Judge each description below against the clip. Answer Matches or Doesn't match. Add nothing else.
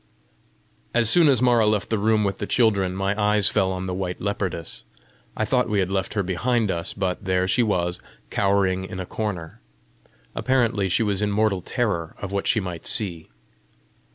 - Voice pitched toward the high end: Doesn't match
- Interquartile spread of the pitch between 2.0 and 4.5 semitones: Matches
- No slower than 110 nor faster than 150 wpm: Doesn't match